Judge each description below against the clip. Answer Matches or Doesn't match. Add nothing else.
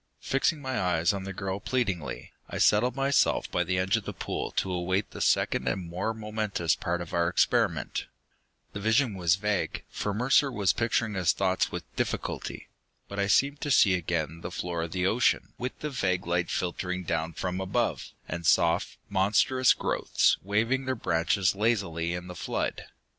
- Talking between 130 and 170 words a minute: Doesn't match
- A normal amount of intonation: Matches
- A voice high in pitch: Doesn't match